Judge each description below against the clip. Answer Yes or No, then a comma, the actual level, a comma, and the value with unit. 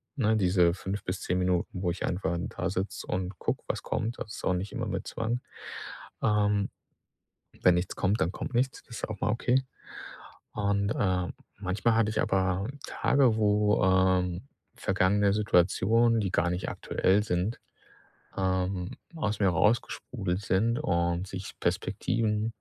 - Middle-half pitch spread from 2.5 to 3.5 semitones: Yes, average, 2.8 semitones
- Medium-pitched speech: No, low, 100 Hz